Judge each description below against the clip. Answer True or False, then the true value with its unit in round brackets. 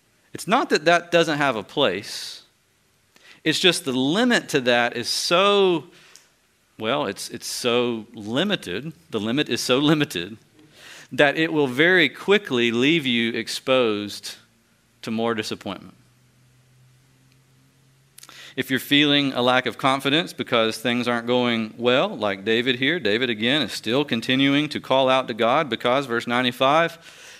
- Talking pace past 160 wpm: False (140 wpm)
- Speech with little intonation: False (3.5 semitones)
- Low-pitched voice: True (130 Hz)